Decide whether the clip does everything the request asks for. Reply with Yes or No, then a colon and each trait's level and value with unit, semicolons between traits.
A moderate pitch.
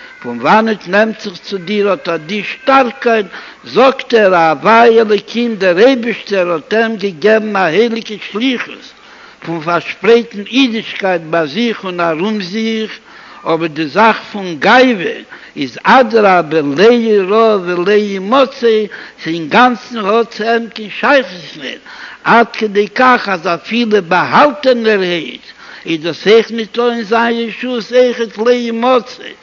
No: high, 220 Hz